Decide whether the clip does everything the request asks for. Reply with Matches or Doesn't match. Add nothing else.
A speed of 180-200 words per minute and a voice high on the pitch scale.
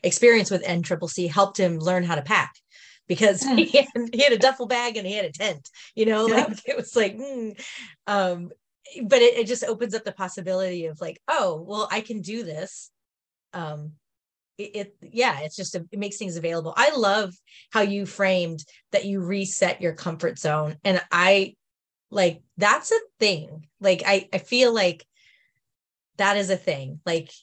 Matches